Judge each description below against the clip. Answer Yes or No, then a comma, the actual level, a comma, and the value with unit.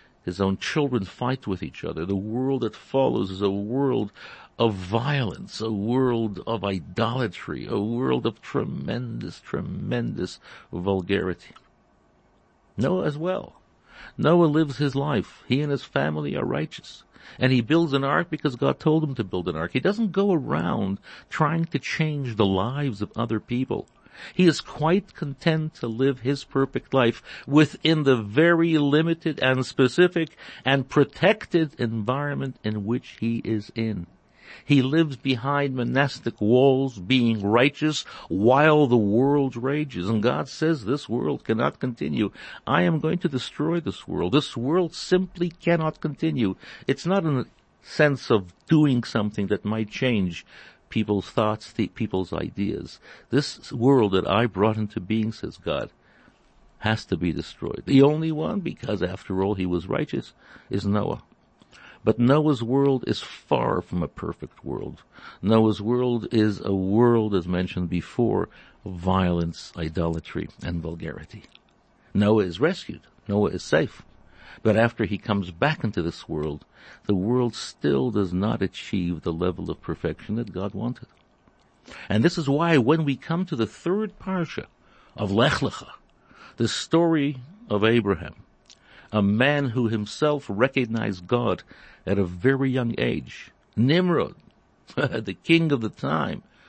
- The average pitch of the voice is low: Yes, low, 120 Hz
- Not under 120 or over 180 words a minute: Yes, average, 150 wpm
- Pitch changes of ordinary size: No, wide, 6.2 semitones